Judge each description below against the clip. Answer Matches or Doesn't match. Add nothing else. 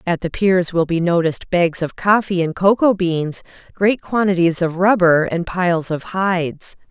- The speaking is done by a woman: Matches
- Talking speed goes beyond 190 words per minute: Doesn't match